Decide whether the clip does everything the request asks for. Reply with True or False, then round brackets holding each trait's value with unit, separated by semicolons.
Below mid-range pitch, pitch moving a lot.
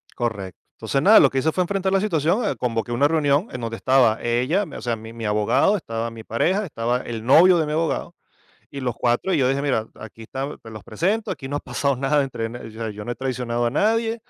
True (130 Hz; 5.8 semitones)